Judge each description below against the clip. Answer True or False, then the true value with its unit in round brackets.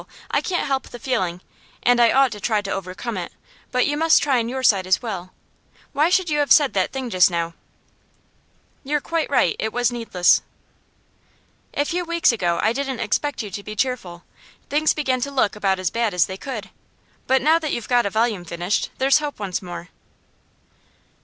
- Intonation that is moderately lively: False (6.4 semitones)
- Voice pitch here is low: False (235 Hz)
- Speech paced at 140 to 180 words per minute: False (200 wpm)